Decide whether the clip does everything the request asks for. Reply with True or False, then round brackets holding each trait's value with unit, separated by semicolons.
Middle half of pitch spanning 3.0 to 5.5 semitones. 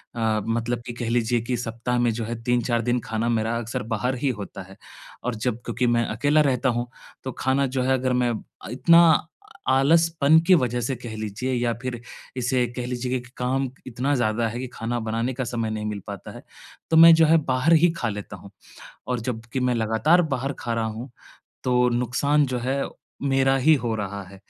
False (2.4 semitones)